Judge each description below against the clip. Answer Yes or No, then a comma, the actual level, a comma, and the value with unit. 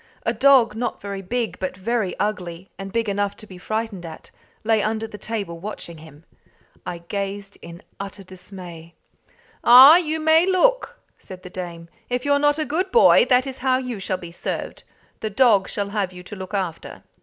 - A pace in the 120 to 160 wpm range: No, average, 190 wpm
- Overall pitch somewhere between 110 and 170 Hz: No, high, 205 Hz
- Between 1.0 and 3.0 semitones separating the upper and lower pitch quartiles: No, average, 5.2 semitones